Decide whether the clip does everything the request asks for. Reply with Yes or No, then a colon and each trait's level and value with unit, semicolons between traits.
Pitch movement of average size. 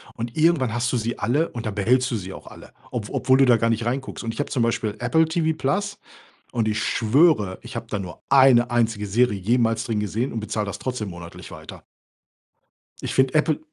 Yes: average, 3.3 semitones